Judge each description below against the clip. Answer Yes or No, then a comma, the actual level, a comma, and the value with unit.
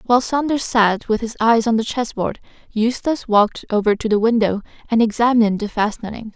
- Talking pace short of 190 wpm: Yes, average, 180 wpm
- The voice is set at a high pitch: Yes, high, 225 Hz